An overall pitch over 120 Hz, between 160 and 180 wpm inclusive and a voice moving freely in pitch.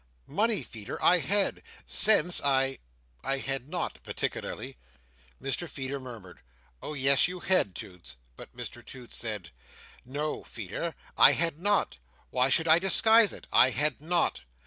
No: medium, 140 Hz; average, 140 wpm; wide, 6.5 semitones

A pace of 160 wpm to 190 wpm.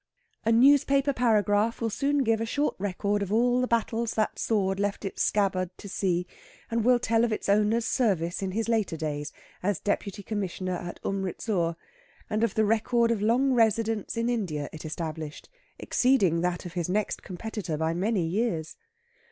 Yes: average, 175 wpm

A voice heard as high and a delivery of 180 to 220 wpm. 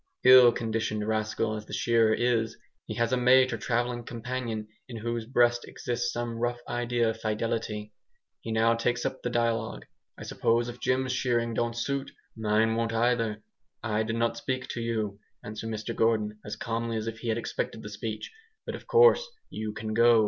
No: low, 115 Hz; average, 185 wpm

